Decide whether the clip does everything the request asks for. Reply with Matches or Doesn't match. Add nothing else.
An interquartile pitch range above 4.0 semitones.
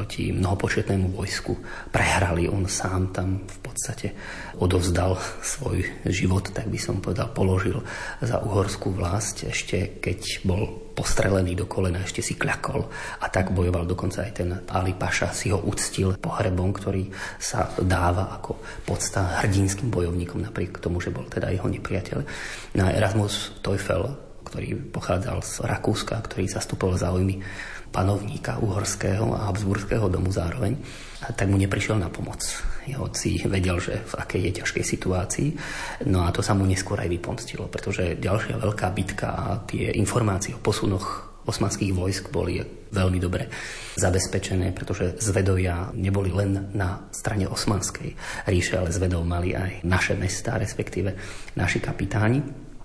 Doesn't match